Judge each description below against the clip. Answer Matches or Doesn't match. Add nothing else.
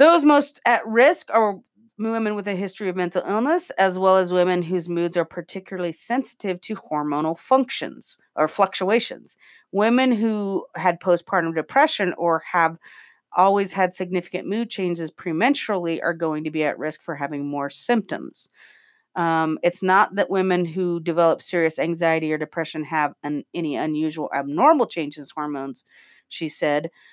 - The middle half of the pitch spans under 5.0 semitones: Matches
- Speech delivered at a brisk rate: Doesn't match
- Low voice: Doesn't match